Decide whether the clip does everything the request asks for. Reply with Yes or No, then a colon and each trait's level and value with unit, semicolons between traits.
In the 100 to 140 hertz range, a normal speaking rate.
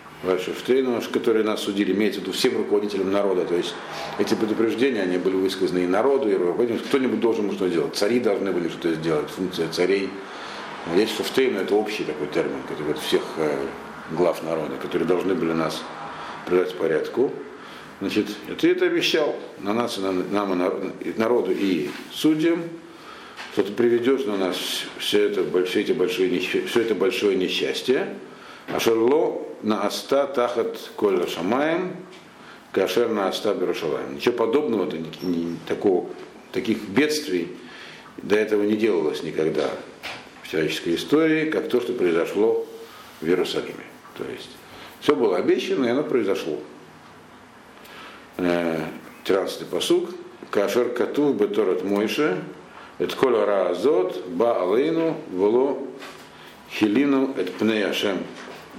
Yes: low, 135 Hz; average, 130 wpm